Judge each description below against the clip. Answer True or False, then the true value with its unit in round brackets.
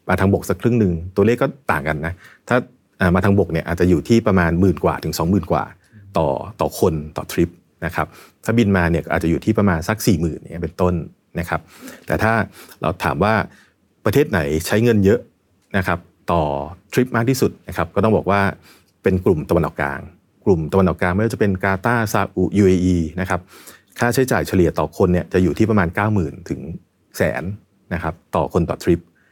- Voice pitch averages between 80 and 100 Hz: True (90 Hz)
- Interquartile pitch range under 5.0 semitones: True (3.3 semitones)